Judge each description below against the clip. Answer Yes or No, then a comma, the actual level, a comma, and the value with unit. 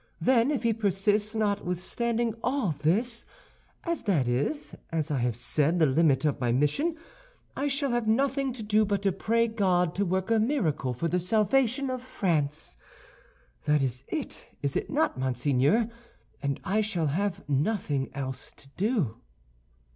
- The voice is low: No, high, 195 Hz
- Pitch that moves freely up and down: Yes, wide, 7.8 semitones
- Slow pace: No, average, 155 wpm